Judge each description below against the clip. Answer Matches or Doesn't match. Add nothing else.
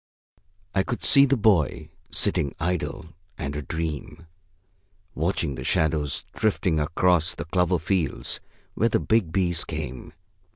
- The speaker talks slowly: Matches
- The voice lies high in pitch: Doesn't match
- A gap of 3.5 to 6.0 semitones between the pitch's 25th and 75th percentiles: Matches